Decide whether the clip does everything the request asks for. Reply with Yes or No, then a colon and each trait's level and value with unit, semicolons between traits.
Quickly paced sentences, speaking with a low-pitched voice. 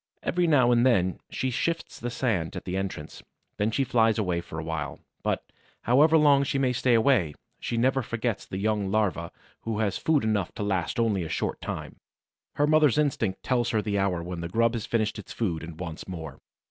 Yes: fast, 210 wpm; low, 110 Hz